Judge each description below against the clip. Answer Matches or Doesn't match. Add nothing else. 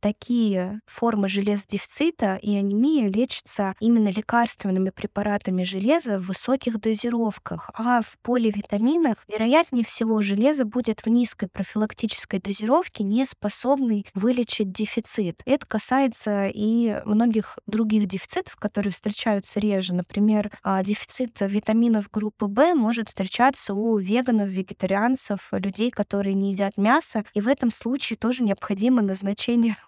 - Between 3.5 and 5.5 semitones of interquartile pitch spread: Doesn't match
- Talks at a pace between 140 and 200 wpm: Doesn't match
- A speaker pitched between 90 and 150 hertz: Doesn't match